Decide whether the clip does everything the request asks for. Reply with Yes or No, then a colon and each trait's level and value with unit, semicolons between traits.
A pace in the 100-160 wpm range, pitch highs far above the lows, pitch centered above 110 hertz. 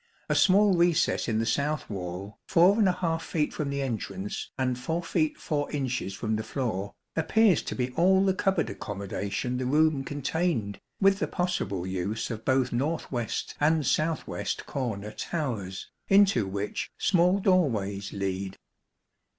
Yes: average, 150 wpm; wide, 8.2 semitones; low, 135 Hz